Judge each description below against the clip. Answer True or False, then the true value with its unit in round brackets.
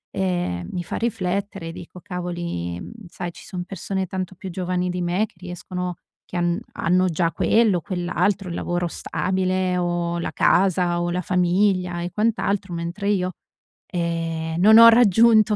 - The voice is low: False (180 Hz)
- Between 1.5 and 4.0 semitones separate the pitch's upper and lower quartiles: True (1.8 semitones)